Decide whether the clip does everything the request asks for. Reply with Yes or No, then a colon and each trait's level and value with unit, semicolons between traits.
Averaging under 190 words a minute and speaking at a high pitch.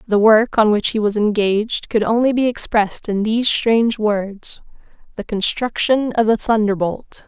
Yes: average, 155 wpm; high, 220 Hz